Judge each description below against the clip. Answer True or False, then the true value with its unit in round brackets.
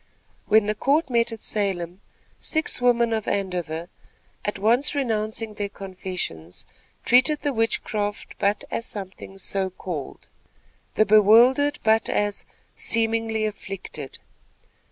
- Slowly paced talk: True (115 wpm)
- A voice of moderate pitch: False (215 Hz)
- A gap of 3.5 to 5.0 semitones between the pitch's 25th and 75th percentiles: False (2.9 semitones)